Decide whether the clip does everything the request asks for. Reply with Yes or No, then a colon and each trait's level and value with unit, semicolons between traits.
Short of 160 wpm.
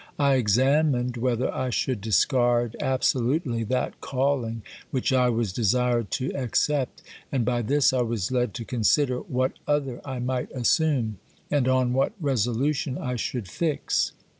Yes: average, 145 wpm